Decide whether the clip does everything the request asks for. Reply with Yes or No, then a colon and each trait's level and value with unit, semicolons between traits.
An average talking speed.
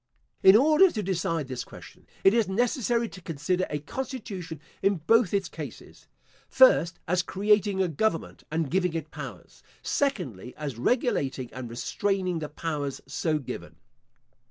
Yes: average, 145 wpm